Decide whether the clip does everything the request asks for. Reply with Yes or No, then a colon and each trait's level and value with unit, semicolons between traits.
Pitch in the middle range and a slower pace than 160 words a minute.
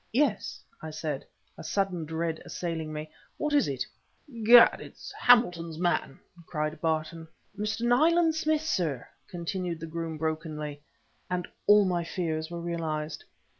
Yes: medium, 170 Hz; slow, 135 wpm